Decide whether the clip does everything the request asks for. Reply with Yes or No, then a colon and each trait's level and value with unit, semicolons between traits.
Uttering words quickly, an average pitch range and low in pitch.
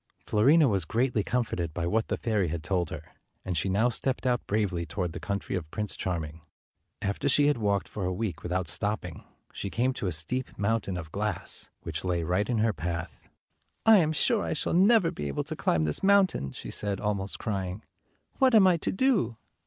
No: fast, 210 wpm; wide, 6.0 semitones; low, 100 Hz